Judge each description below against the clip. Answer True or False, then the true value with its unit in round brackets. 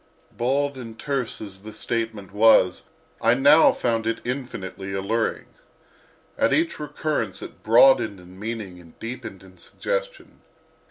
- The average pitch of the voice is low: True (115 Hz)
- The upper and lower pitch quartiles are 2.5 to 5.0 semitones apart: False (5.4 semitones)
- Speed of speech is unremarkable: False (130 wpm)